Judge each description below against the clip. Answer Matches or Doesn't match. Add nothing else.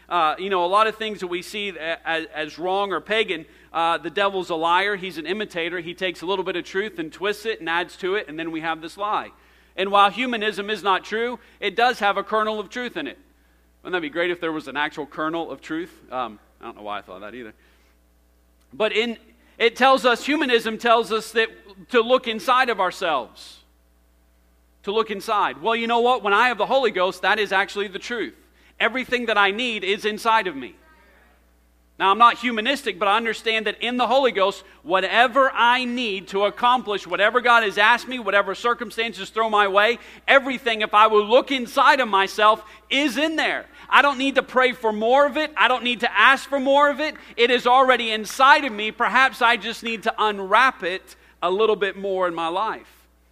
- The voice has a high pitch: Matches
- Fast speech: Matches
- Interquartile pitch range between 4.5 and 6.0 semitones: Matches